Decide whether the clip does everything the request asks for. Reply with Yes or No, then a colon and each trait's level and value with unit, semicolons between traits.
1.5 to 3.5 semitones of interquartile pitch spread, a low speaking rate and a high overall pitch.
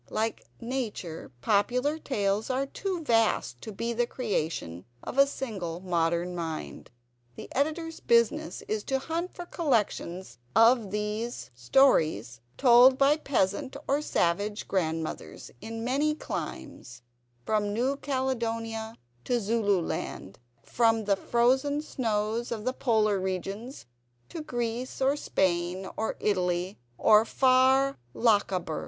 No: wide, 5.6 semitones; slow, 120 wpm; high, 225 Hz